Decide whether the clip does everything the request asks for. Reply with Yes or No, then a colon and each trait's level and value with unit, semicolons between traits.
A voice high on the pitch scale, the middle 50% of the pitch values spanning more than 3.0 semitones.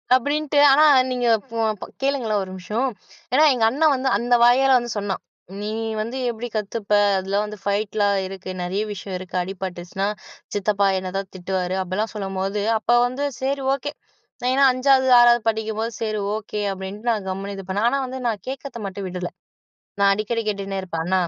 Yes: high, 210 Hz; average, 3.9 semitones